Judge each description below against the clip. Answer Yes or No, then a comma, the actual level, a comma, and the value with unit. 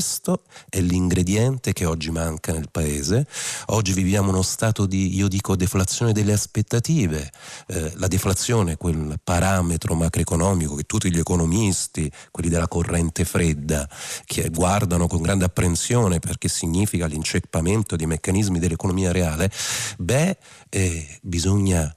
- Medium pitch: No, very low, 90 Hz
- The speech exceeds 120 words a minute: Yes, average, 130 wpm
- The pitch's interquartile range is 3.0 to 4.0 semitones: Yes, average, 3.3 semitones